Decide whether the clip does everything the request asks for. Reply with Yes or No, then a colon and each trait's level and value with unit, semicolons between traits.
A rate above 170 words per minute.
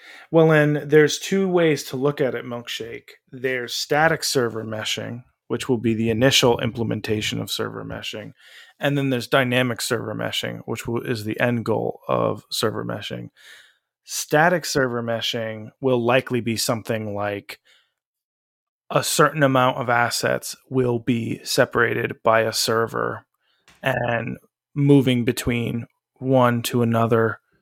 No: slow, 135 wpm